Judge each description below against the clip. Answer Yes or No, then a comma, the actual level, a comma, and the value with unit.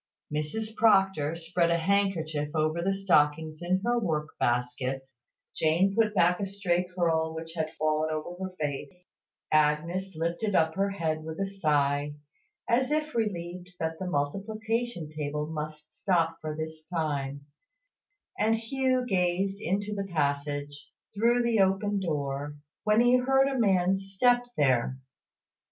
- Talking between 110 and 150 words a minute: Yes, average, 140 wpm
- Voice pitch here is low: No, medium, 175 Hz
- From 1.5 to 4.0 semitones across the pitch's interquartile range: No, average, 4.5 semitones